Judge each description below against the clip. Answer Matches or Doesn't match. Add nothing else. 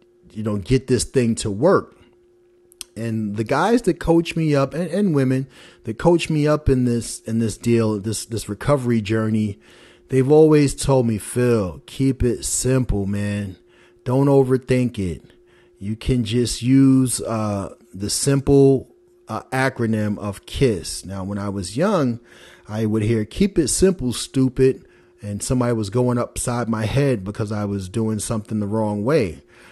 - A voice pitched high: Doesn't match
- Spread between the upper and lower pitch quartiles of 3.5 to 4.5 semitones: Matches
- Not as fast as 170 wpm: Matches